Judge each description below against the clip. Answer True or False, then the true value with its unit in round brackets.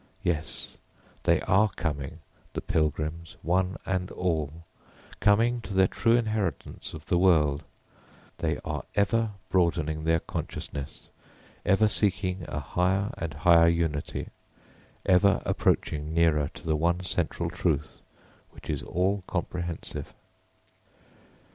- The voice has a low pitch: True (85 Hz)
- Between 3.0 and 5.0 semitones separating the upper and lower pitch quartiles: True (3.4 semitones)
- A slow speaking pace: True (115 wpm)